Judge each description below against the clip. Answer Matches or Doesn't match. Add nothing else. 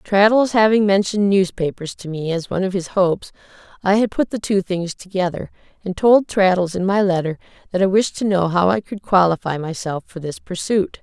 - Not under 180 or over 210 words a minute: Matches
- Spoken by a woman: Matches